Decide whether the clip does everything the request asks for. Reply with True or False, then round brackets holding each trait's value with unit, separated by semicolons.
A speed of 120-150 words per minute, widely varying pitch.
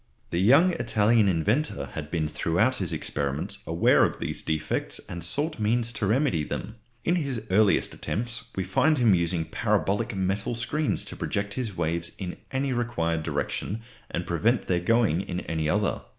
False (165 wpm; 5.9 semitones)